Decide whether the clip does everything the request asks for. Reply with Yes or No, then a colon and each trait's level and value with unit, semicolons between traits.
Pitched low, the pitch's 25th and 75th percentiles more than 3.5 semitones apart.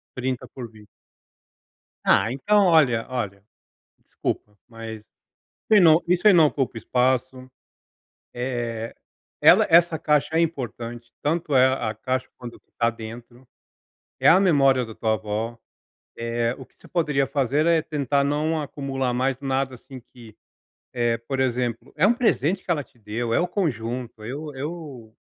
Yes: low, 130 Hz; average, 4.3 semitones